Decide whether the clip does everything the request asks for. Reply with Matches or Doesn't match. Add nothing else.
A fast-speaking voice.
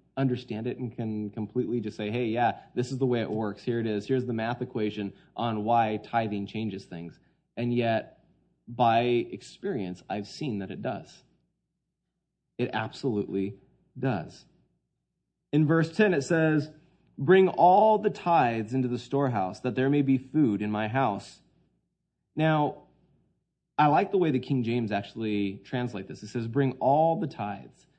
Doesn't match